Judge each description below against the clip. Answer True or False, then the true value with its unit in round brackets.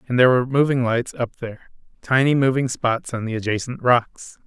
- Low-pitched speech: True (125 Hz)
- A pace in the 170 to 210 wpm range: True (190 wpm)